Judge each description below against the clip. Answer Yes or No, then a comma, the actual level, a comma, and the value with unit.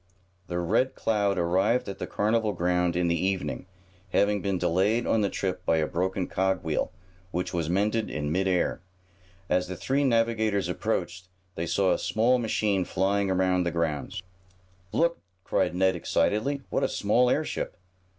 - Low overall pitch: Yes, very low, 95 Hz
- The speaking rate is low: No, average, 165 wpm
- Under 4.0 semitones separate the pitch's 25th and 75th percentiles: Yes, average, 3.4 semitones